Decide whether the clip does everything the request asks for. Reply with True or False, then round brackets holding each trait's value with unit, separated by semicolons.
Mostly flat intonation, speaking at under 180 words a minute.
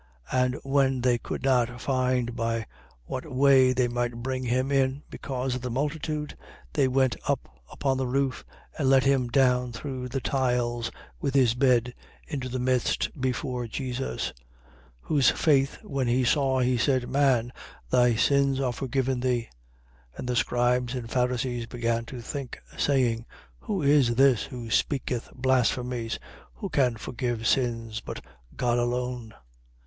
True (1.8 semitones; 155 wpm)